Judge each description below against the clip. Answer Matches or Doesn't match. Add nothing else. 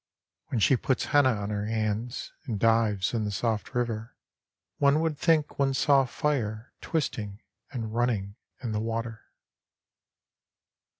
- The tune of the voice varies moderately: Matches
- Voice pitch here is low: Matches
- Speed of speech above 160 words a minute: Doesn't match